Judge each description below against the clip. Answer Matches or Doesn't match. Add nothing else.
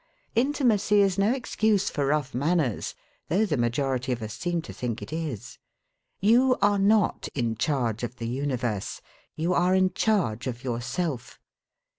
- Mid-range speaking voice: Matches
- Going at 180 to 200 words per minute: Doesn't match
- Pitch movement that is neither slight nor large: Doesn't match